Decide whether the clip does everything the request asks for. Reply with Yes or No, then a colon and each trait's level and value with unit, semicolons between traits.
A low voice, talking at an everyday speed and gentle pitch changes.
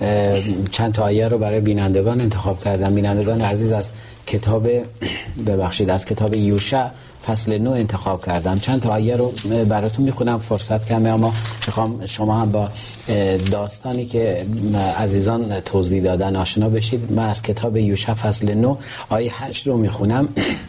Yes: low, 110 Hz; average, 145 wpm; narrow, 2.1 semitones